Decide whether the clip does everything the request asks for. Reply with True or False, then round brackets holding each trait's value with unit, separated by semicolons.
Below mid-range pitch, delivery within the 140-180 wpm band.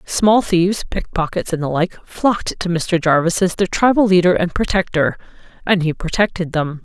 False (180 Hz; 175 wpm)